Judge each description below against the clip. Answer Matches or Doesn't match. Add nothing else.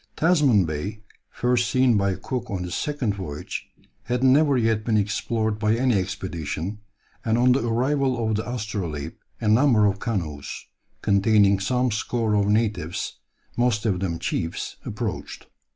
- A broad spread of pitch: Doesn't match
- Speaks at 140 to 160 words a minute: Matches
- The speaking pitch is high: Doesn't match